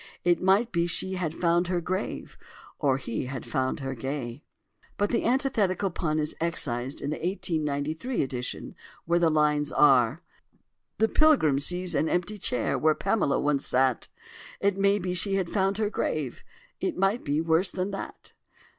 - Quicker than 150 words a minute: Yes, average, 165 wpm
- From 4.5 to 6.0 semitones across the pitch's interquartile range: Yes, average, 5.2 semitones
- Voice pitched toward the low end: No, medium, 170 Hz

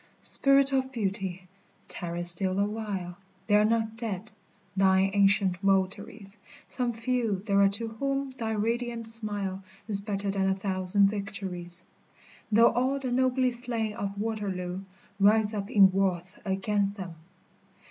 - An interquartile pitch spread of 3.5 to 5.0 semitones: No, average, 3.0 semitones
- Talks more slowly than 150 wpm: Yes, average, 140 wpm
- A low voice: No, high, 205 Hz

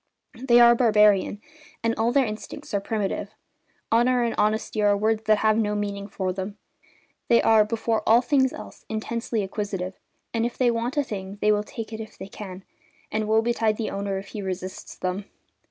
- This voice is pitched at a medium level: No, high, 215 Hz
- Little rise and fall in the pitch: Yes, narrow, 2.2 semitones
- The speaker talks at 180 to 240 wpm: Yes, average, 190 wpm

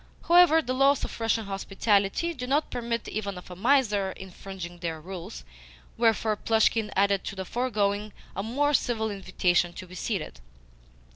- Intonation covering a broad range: No, average, 4.0 semitones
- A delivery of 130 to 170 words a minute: Yes, average, 155 wpm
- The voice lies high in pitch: Yes, high, 210 Hz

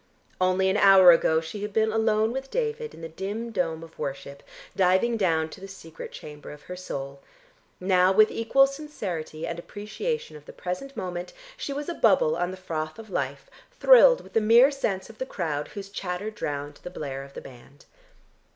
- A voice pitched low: No, medium, 185 Hz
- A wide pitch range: Yes, wide, 5.7 semitones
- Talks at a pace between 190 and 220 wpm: Yes, average, 195 wpm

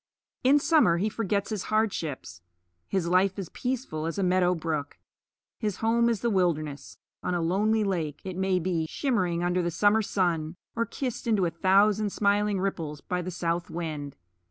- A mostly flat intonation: No, average, 4.0 semitones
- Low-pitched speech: No, medium, 185 Hz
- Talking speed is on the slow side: No, average, 175 wpm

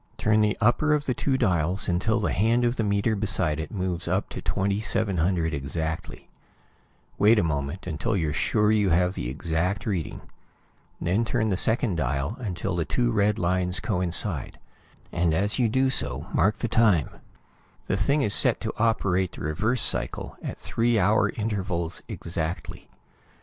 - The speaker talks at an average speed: Yes, average, 165 wpm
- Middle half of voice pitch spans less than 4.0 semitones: No, average, 4.5 semitones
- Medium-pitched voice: No, very low, 95 Hz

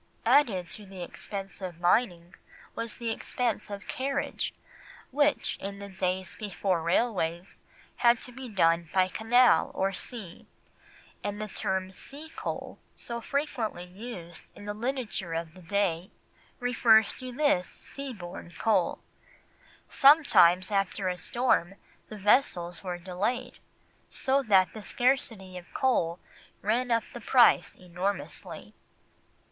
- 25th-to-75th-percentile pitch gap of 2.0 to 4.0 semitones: No, average, 5.1 semitones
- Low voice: No, high, 200 Hz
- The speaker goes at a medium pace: No, slow, 130 wpm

